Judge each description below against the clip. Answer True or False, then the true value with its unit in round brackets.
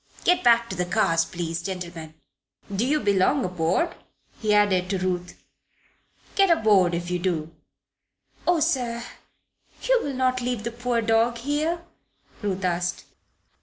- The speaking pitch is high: True (210 Hz)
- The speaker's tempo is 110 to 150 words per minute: True (140 wpm)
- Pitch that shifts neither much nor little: False (5.7 semitones)